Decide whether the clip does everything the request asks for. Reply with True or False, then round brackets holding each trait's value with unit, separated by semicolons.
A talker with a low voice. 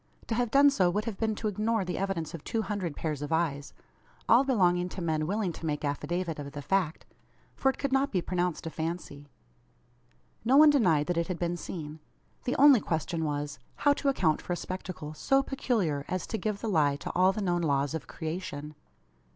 False (180 Hz)